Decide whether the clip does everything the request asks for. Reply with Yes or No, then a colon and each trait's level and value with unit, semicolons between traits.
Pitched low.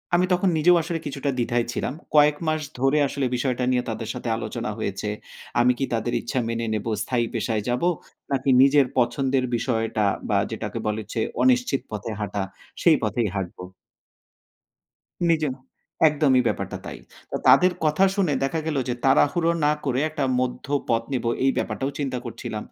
Yes: low, 130 Hz